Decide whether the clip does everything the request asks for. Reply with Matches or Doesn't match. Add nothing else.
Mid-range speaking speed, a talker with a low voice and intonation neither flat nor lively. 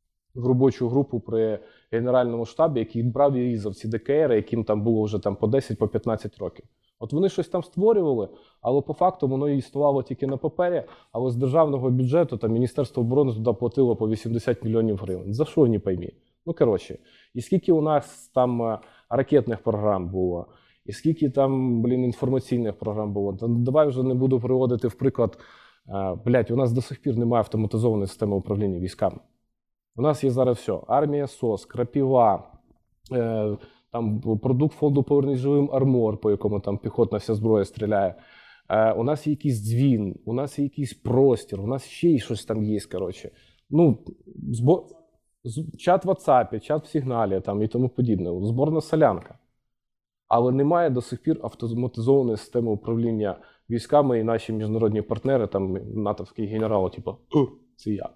Doesn't match